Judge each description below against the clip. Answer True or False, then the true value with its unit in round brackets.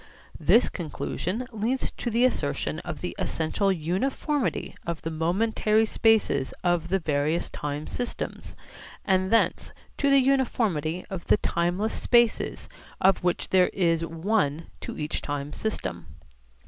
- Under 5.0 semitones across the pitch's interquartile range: False (5.5 semitones)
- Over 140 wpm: False (135 wpm)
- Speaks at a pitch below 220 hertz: True (185 Hz)